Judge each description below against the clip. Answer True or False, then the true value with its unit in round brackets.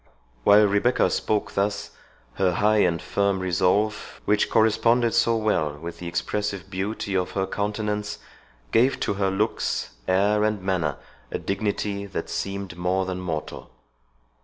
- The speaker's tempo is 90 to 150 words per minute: True (140 wpm)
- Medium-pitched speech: False (100 Hz)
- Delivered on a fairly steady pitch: True (2.3 semitones)